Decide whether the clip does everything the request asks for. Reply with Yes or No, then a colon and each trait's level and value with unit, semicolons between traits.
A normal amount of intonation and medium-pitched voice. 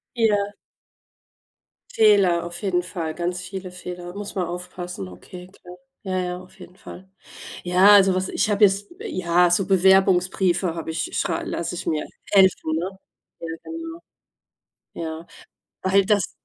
No: narrow, 1.9 semitones; medium, 180 Hz